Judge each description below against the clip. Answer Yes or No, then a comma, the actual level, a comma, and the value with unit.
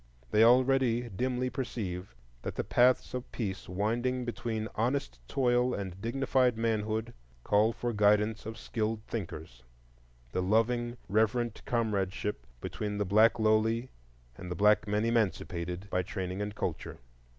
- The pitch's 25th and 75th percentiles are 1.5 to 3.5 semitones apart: Yes, average, 2.8 semitones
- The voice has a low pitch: Yes, low, 110 Hz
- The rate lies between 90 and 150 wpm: Yes, average, 140 wpm